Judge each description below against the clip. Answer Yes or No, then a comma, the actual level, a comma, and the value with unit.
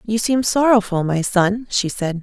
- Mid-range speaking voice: No, high, 210 Hz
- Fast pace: No, average, 190 wpm